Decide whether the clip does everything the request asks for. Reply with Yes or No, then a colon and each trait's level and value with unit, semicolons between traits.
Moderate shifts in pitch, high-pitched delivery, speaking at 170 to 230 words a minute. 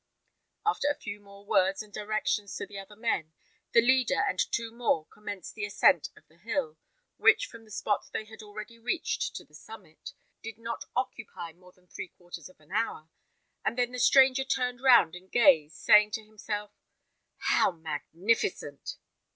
Yes: average, 4.3 semitones; high, 210 Hz; average, 175 wpm